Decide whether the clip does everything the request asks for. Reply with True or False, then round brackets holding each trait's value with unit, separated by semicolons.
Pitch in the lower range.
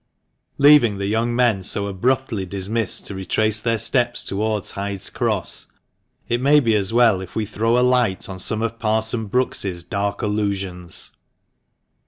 True (110 Hz)